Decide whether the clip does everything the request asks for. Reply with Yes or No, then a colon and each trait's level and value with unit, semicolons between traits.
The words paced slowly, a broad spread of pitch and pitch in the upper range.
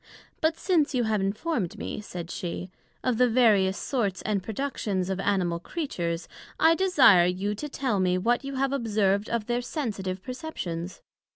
No: average, 165 wpm; wide, 5.8 semitones; high, 210 Hz